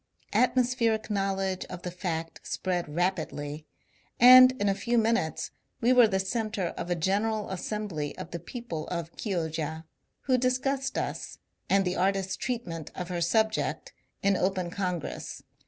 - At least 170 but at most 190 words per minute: No, average, 155 wpm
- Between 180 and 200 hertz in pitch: Yes, high, 190 Hz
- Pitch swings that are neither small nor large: Yes, average, 4.6 semitones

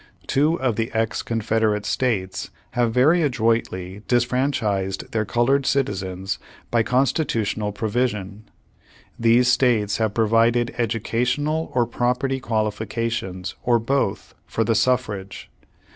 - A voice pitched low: Yes, low, 115 Hz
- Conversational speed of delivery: No, slow, 115 wpm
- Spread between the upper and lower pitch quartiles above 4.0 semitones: No, average, 3.2 semitones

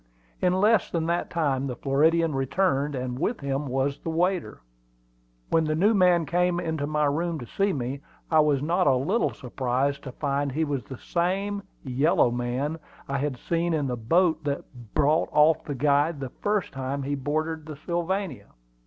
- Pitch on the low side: No, medium, 150 Hz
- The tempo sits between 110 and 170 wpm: No, average, 180 wpm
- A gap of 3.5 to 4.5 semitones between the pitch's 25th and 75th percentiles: Yes, average, 3.9 semitones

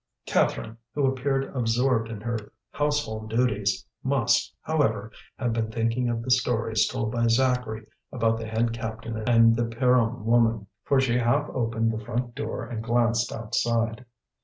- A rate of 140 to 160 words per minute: Yes, average, 155 wpm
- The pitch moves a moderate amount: No, narrow, 1.8 semitones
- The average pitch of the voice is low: Yes, low, 115 Hz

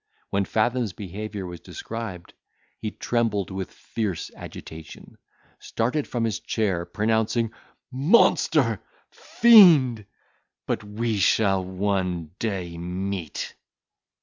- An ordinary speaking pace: No, slow, 95 wpm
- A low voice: Yes, low, 105 Hz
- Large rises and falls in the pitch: No, average, 3.6 semitones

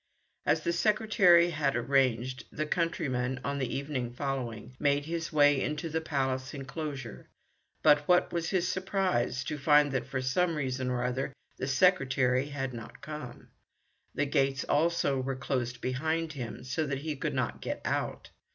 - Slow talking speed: No, average, 160 wpm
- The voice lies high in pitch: No, medium, 140 Hz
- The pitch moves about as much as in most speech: Yes, average, 3.5 semitones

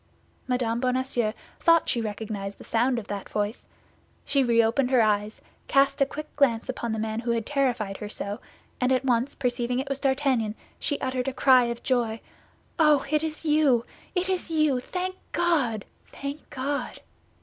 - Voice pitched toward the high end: Yes, very high, 250 Hz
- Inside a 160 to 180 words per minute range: Yes, average, 170 wpm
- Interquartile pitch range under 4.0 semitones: Yes, average, 3.6 semitones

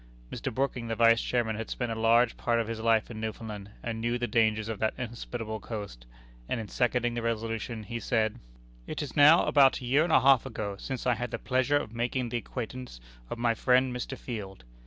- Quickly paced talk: Yes, fast, 220 wpm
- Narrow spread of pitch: Yes, narrow, 2.0 semitones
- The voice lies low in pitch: Yes, low, 115 Hz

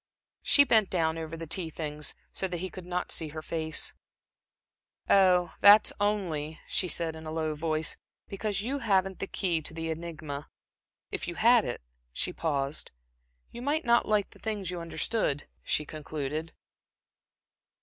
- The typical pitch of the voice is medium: Yes, medium, 170 Hz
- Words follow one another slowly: No, average, 160 wpm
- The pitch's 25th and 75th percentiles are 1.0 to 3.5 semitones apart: No, average, 3.9 semitones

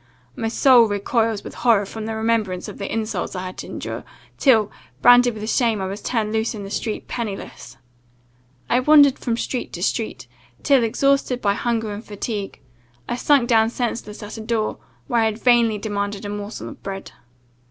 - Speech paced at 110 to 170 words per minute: No, average, 185 wpm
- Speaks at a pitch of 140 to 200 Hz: No, high, 220 Hz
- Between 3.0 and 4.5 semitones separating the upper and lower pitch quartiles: No, narrow, 2.6 semitones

